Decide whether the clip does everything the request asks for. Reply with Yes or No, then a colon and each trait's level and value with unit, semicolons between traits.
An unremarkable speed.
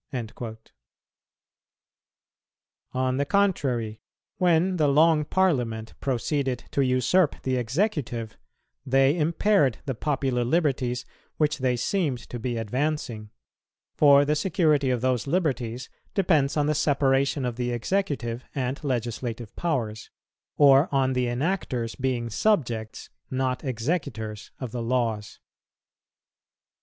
No: slow, 115 wpm